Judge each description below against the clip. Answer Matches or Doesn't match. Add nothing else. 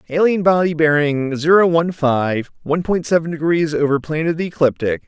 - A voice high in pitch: Doesn't match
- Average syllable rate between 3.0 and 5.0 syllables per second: Doesn't match